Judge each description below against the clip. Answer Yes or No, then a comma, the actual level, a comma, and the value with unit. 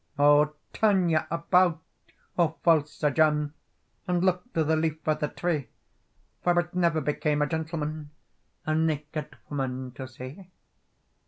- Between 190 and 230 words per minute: No, average, 145 wpm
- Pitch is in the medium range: Yes, medium, 155 Hz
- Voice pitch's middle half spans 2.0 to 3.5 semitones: Yes, narrow, 2.4 semitones